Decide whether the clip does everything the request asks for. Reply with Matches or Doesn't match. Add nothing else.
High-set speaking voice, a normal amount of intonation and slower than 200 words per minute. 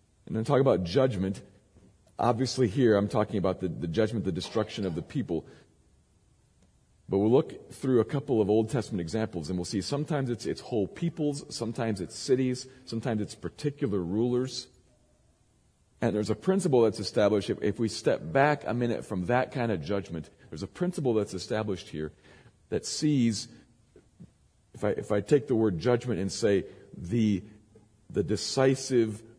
Doesn't match